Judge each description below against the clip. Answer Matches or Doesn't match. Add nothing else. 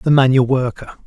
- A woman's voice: Doesn't match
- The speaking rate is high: Doesn't match